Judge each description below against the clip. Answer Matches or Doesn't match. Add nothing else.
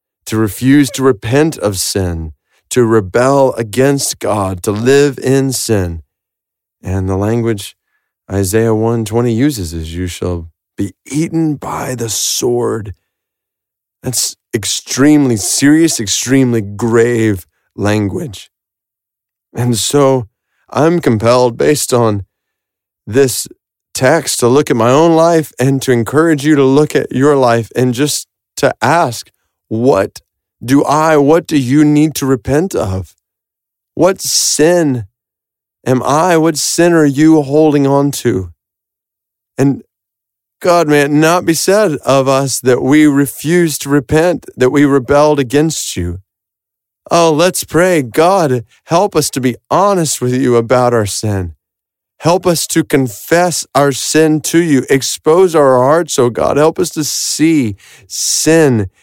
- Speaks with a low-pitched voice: Matches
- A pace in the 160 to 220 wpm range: Doesn't match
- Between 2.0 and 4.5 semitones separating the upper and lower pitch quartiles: Doesn't match